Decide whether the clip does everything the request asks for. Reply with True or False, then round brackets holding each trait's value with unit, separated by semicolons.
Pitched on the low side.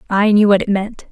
False (205 Hz)